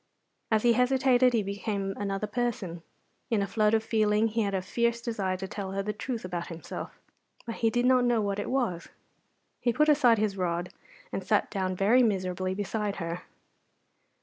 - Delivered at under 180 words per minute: No, average, 185 wpm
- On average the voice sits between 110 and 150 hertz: No, high, 210 Hz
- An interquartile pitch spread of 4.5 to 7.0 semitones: No, average, 3.5 semitones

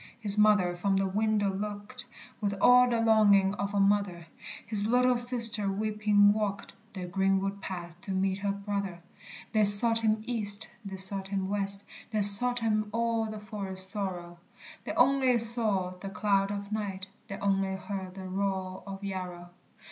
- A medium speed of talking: Yes, average, 165 wpm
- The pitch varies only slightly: Yes, narrow, 2.0 semitones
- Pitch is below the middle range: No, high, 200 Hz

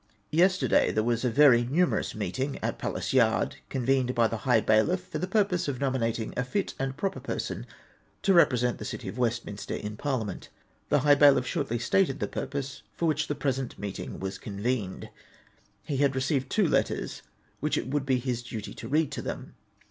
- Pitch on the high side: No, low, 130 Hz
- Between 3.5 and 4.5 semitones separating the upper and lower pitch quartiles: Yes, average, 3.8 semitones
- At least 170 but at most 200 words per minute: Yes, average, 190 wpm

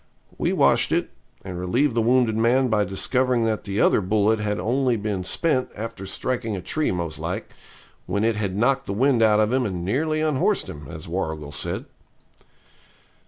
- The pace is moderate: Yes, average, 180 wpm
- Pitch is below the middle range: Yes, low, 110 Hz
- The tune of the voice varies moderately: Yes, average, 4.7 semitones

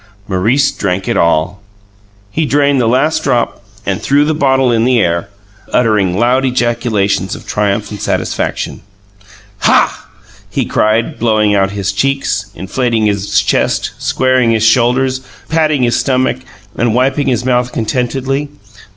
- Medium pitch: No, low, 120 Hz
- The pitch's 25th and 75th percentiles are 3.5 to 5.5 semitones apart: Yes, average, 4.2 semitones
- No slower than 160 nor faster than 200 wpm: No, average, 140 wpm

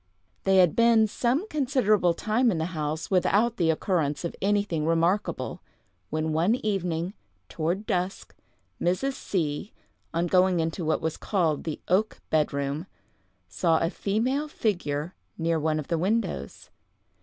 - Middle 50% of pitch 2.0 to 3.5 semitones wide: No, average, 4.6 semitones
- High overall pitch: No, medium, 180 Hz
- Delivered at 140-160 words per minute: Yes, average, 145 wpm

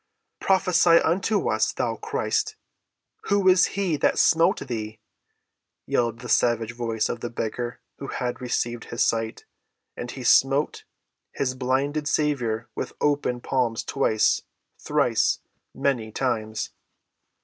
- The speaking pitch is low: Yes, low, 125 Hz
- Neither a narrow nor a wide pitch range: Yes, average, 4.2 semitones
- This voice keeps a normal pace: No, slow, 115 wpm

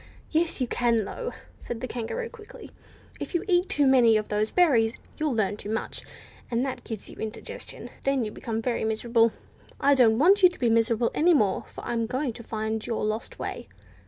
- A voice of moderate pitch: No, high, 235 Hz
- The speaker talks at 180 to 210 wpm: Yes, average, 200 wpm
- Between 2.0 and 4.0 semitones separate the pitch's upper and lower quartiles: No, average, 4.5 semitones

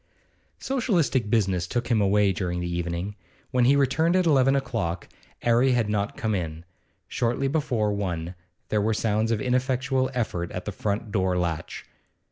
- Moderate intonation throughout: No, wide, 5.9 semitones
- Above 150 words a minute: Yes, average, 165 wpm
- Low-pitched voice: Yes, low, 110 Hz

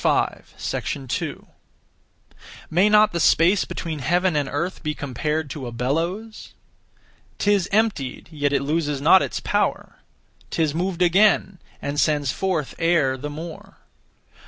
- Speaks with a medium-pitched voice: Yes, medium, 165 Hz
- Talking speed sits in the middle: No, slow, 125 wpm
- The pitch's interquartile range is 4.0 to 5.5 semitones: Yes, average, 4.3 semitones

